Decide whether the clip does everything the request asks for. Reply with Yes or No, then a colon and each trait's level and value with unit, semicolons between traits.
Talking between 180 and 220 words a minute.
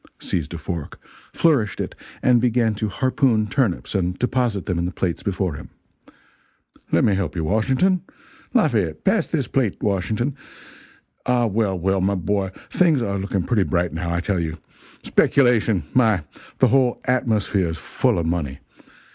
No: average, 160 wpm